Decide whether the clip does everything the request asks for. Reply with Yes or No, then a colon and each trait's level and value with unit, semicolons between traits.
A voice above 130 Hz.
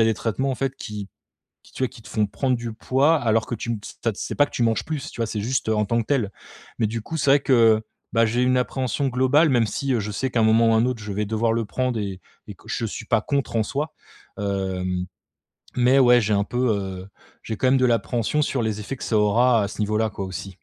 No: low, 115 Hz